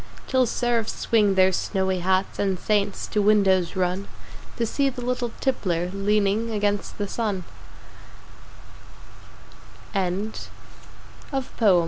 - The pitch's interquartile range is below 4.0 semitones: Yes, average, 3.2 semitones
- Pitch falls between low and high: No, high, 205 Hz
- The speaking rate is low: Yes, slow, 110 wpm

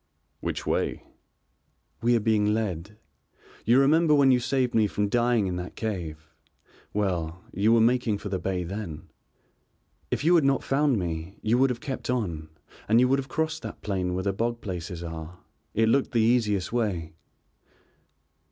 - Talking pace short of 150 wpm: No, average, 170 wpm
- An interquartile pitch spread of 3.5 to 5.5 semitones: Yes, average, 5.2 semitones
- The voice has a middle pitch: No, low, 110 Hz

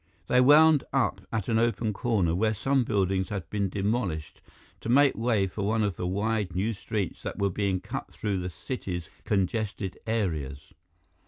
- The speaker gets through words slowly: No, average, 170 wpm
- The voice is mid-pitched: No, low, 105 Hz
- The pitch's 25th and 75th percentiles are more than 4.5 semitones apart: No, average, 3.4 semitones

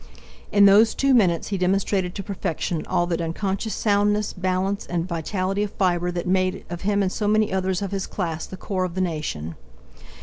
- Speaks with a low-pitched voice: No, medium, 185 Hz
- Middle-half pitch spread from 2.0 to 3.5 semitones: Yes, narrow, 2.4 semitones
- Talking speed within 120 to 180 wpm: No, average, 195 wpm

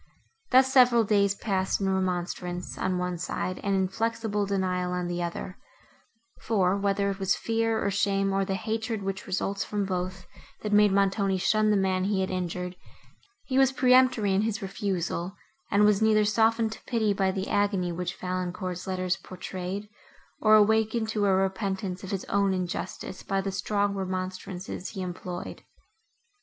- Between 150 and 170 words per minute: Yes, average, 165 wpm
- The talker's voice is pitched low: No, high, 195 Hz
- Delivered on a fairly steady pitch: Yes, narrow, 2.3 semitones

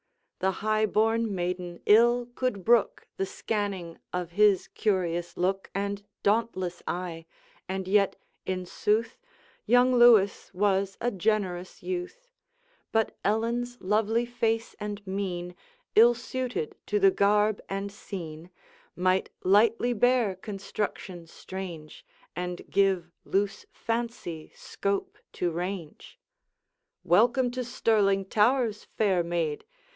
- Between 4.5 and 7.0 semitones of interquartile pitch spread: No, average, 3.9 semitones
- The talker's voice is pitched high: Yes, high, 200 Hz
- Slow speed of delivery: Yes, slow, 115 wpm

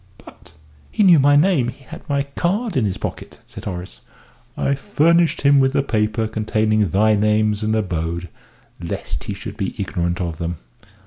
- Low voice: Yes, low, 110 Hz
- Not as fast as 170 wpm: No, average, 175 wpm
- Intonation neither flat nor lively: No, wide, 5.9 semitones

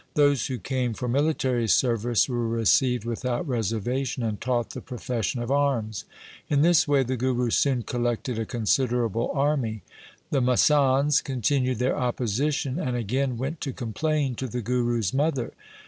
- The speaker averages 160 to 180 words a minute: No, average, 150 wpm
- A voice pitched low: Yes, low, 125 Hz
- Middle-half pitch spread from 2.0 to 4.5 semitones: Yes, average, 2.7 semitones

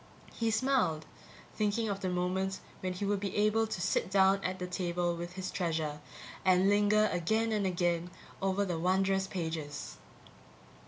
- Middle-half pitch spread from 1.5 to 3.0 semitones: Yes, narrow, 2.6 semitones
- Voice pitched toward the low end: No, high, 190 Hz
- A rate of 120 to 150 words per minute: No, average, 160 wpm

